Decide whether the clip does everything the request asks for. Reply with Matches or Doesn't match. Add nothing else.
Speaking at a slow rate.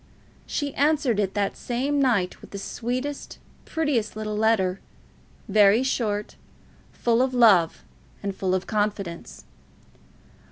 Matches